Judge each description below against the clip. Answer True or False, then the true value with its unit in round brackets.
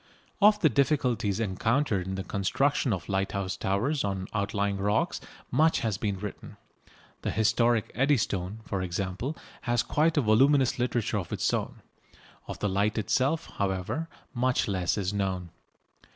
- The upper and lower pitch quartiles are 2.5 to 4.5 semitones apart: False (4.9 semitones)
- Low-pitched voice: True (105 Hz)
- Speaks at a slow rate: False (145 wpm)